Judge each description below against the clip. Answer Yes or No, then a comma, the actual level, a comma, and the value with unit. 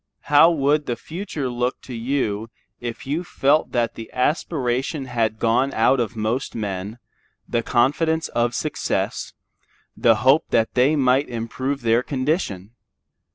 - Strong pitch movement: No, average, 3.6 semitones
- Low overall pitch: Yes, low, 125 Hz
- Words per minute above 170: No, average, 140 wpm